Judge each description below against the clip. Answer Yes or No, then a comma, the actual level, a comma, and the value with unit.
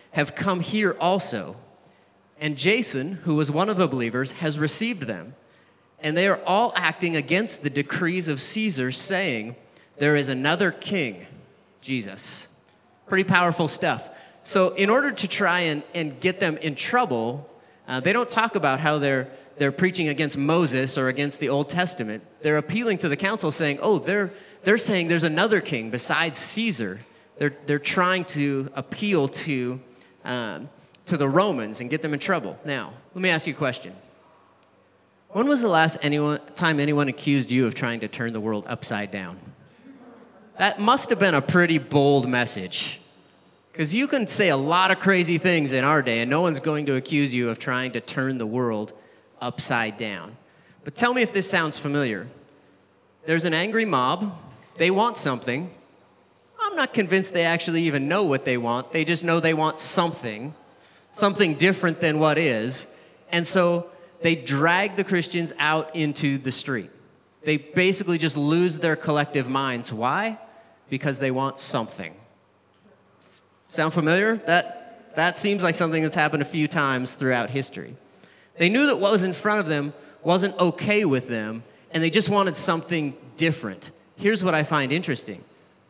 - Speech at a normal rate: Yes, average, 170 wpm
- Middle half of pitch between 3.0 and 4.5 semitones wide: No, average, 5.3 semitones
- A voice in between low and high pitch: Yes, medium, 160 Hz